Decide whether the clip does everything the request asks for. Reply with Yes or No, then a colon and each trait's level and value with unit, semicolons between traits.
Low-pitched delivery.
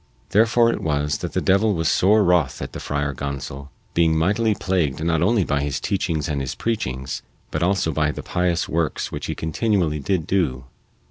Yes: very low, 80 Hz